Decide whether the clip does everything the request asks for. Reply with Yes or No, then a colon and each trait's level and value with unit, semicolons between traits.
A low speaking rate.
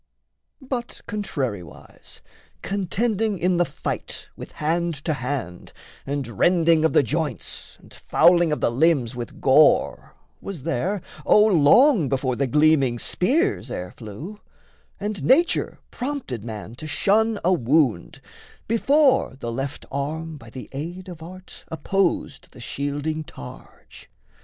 Yes: slow, 130 wpm